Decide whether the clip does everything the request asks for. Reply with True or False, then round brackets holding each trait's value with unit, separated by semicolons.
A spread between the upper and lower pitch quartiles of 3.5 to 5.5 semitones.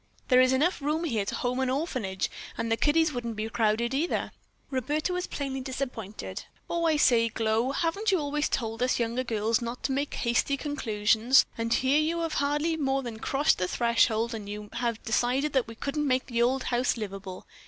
True (4.2 semitones)